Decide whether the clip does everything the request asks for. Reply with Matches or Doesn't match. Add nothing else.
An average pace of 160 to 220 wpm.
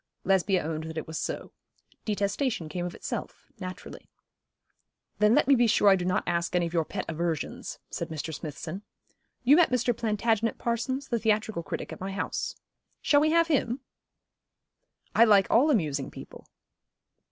Matches